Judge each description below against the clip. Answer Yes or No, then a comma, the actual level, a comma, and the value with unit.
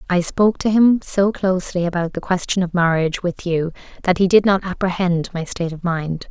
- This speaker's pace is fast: Yes, fast, 210 wpm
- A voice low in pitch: No, medium, 180 Hz